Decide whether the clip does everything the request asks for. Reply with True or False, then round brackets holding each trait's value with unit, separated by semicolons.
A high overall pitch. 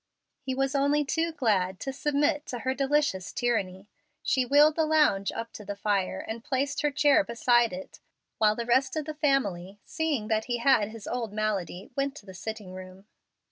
True (240 Hz)